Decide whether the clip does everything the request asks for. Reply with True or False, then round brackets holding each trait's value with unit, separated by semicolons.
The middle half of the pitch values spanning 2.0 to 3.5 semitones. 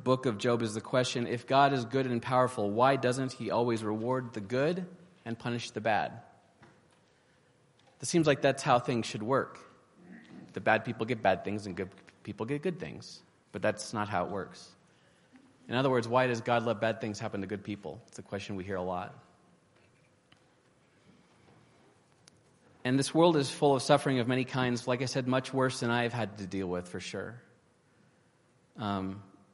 False (4.1 semitones)